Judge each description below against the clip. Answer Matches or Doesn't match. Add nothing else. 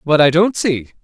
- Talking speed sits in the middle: Doesn't match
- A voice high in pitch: Doesn't match